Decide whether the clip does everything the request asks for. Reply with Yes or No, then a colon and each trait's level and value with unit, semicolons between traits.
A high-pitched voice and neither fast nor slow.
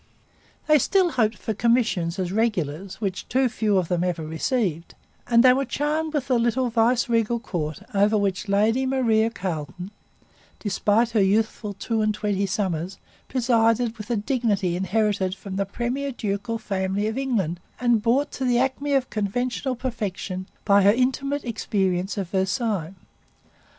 Yes: high, 215 Hz; average, 155 wpm